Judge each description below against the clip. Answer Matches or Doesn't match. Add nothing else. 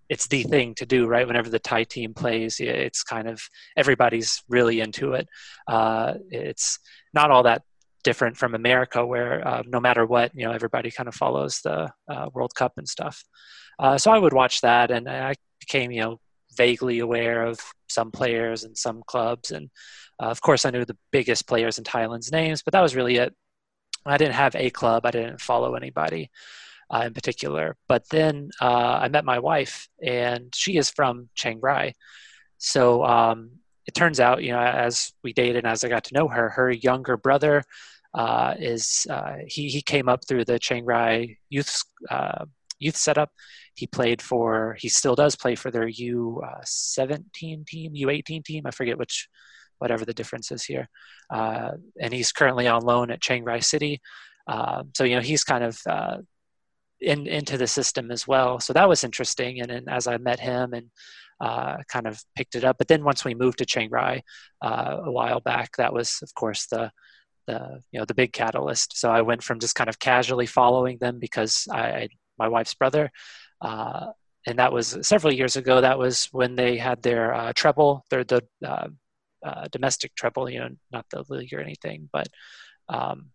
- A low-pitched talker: Matches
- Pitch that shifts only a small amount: Matches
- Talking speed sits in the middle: Matches